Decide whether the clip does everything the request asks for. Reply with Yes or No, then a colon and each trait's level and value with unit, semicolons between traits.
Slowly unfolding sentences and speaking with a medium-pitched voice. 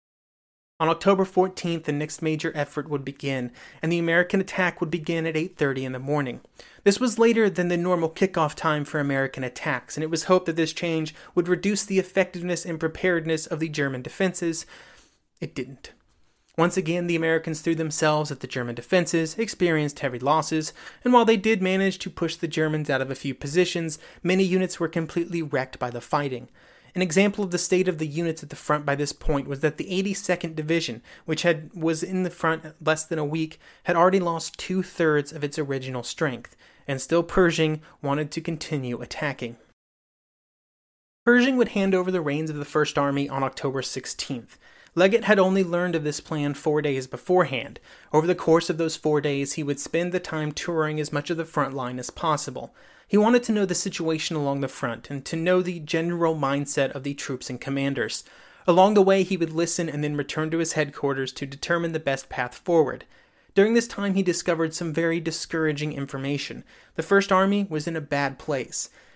No: average, 200 wpm; medium, 160 Hz